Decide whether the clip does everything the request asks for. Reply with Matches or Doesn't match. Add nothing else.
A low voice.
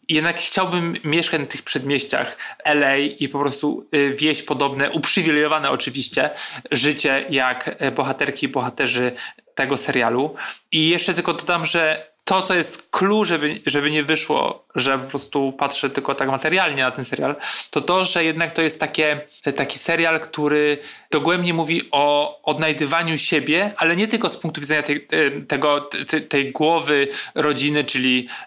Doesn't match